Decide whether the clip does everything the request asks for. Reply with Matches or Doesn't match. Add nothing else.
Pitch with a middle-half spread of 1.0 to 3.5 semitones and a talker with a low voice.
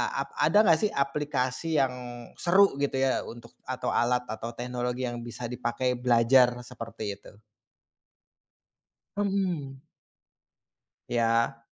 Matches